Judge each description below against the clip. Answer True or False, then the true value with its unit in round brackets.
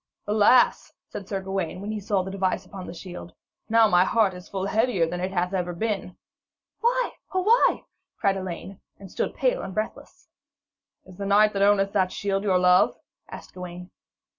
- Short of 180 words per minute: False (185 wpm)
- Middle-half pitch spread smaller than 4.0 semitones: True (2.4 semitones)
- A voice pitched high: True (195 Hz)